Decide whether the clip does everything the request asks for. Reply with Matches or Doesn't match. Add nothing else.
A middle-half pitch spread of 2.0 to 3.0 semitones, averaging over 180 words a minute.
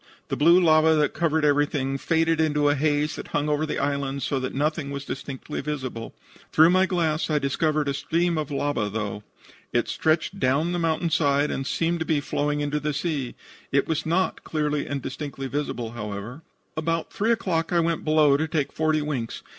Matches